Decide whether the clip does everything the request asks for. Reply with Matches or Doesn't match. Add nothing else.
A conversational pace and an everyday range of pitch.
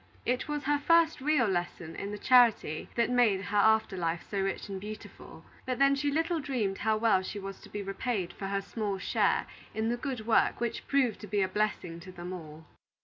Doesn't match